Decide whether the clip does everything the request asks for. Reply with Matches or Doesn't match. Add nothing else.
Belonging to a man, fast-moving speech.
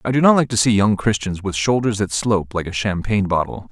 Matches